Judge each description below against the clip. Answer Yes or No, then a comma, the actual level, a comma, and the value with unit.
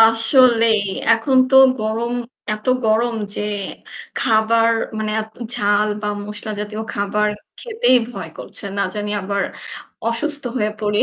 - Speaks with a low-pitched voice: No, high, 220 Hz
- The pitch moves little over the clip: Yes, narrow, 1.8 semitones